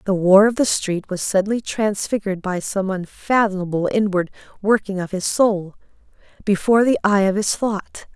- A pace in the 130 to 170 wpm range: Yes, average, 160 wpm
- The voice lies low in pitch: No, high, 200 Hz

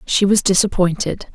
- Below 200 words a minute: Yes, slow, 135 wpm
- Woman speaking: Yes, female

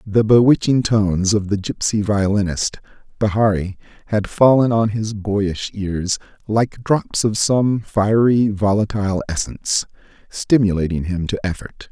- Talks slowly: Yes, slow, 125 wpm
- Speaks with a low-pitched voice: Yes, low, 105 Hz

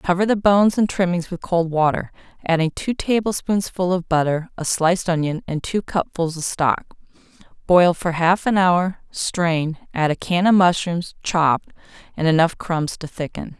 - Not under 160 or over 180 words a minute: Yes, average, 170 wpm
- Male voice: No, female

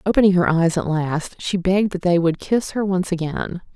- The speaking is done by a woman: Yes, female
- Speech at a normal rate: No, fast, 225 wpm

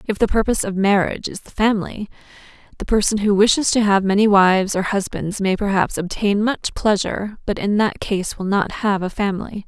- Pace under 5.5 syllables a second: No, 5.6 syllables/s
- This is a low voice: No, high, 200 Hz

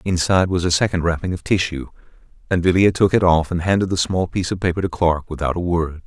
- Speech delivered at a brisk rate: Yes, fast, 240 wpm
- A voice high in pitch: No, very low, 85 Hz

